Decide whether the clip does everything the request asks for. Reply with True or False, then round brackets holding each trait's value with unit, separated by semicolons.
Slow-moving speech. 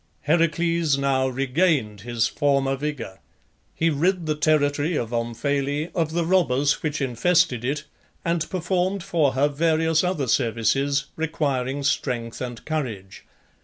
True (130 wpm)